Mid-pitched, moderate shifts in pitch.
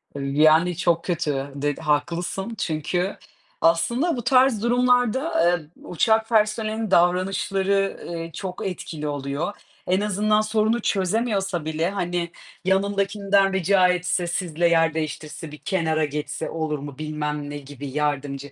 Yes: medium, 175 Hz; average, 4.6 semitones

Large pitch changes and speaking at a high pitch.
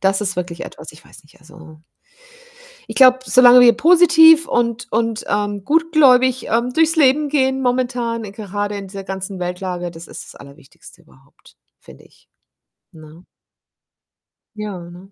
Yes: wide, 6.2 semitones; high, 215 Hz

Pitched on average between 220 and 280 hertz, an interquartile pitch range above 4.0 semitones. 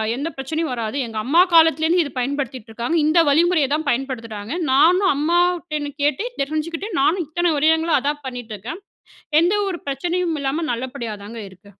No: very high, 295 Hz; average, 4.6 semitones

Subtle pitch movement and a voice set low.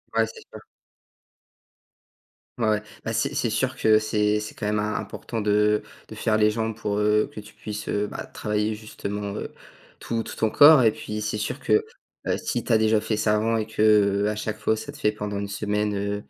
Yes: narrow, 0.9 semitones; low, 105 Hz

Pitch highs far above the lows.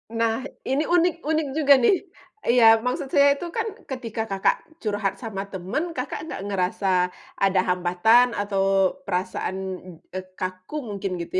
Yes: wide, 6.0 semitones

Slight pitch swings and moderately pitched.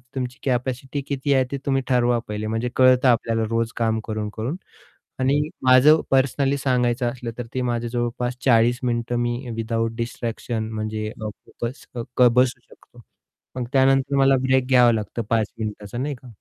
No: narrow, 2.3 semitones; low, 120 Hz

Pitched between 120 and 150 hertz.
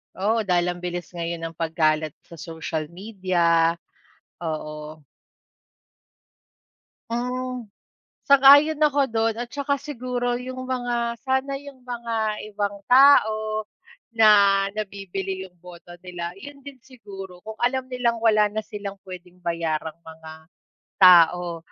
No: high, 210 Hz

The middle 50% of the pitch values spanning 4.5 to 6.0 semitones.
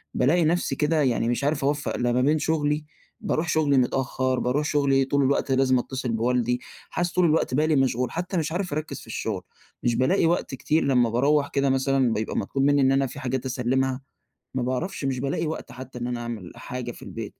No: average, 3.1 semitones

